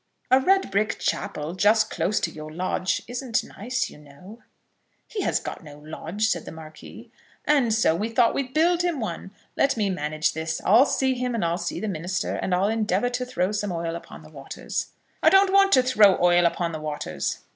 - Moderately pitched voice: No, high, 205 Hz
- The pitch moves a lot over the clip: Yes, wide, 6.8 semitones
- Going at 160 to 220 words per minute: Yes, fast, 205 wpm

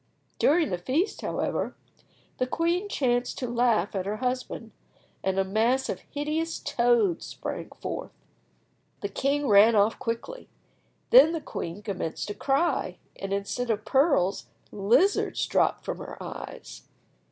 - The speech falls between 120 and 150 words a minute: Yes, average, 140 wpm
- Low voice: No, high, 240 Hz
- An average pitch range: No, wide, 6.2 semitones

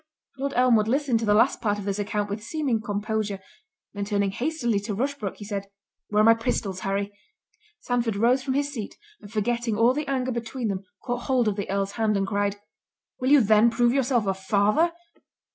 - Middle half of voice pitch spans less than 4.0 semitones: Yes, average, 3.5 semitones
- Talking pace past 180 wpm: Yes, average, 195 wpm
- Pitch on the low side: No, high, 220 Hz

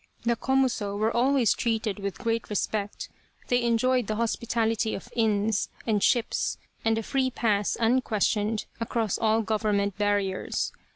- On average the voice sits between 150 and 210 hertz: No, high, 225 Hz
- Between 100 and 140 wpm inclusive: Yes, slow, 135 wpm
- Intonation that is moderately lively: No, narrow, 2.3 semitones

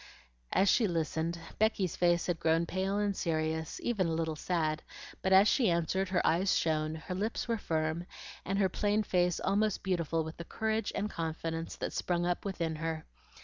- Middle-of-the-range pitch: Yes, medium, 175 Hz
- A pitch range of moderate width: Yes, average, 3.2 semitones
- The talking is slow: No, average, 185 wpm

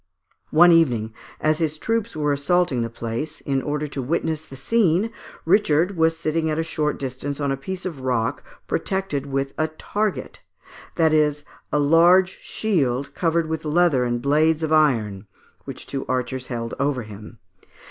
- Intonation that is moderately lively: Yes, average, 3.8 semitones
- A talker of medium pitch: Yes, medium, 150 Hz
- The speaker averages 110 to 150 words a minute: No, average, 165 wpm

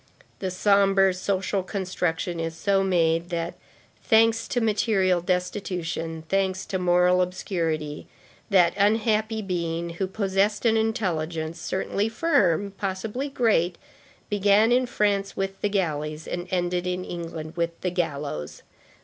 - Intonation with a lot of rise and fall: No, average, 3.2 semitones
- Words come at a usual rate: No, slow, 125 wpm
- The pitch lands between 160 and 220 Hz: Yes, medium, 185 Hz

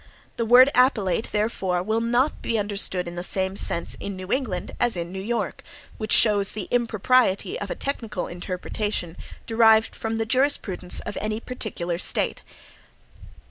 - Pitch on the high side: Yes, high, 215 Hz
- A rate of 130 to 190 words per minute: Yes, average, 155 wpm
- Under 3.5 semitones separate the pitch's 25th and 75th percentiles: No, average, 3.9 semitones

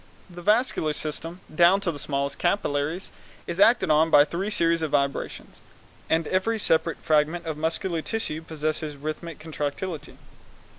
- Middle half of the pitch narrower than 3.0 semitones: Yes, narrow, 2.6 semitones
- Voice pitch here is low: No, medium, 160 Hz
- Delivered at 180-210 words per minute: No, average, 145 wpm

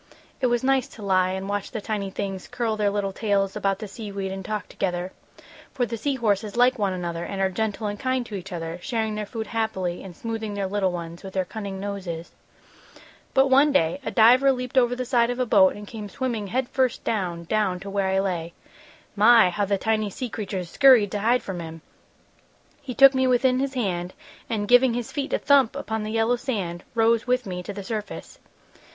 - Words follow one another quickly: Yes, fast, 220 wpm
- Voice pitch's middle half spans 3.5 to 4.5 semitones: Yes, average, 4.0 semitones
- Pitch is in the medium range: No, high, 210 Hz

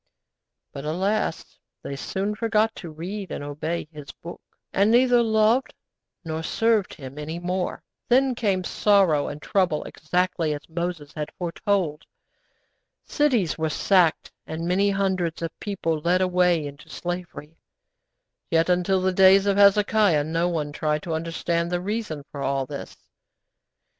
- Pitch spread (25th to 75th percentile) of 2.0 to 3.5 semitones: No, average, 4.1 semitones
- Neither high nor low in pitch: Yes, medium, 175 Hz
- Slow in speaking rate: No, average, 145 wpm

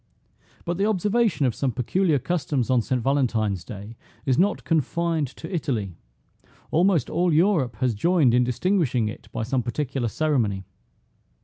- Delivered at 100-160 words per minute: Yes, average, 145 wpm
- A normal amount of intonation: No, wide, 6.2 semitones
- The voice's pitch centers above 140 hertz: No, low, 135 Hz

